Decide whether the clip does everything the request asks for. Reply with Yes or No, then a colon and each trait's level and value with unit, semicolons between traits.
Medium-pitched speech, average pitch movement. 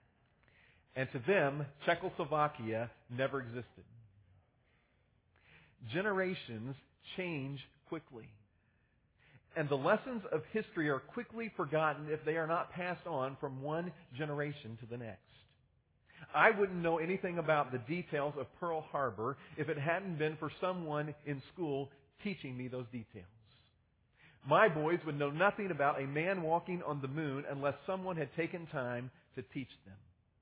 Yes: medium, 145 Hz; average, 5.0 semitones